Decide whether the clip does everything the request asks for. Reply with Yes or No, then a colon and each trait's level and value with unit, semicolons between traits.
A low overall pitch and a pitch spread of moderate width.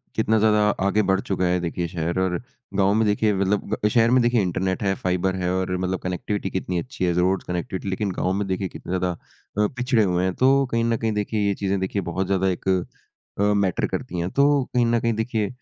Yes: very low, 95 Hz; average, 3.0 semitones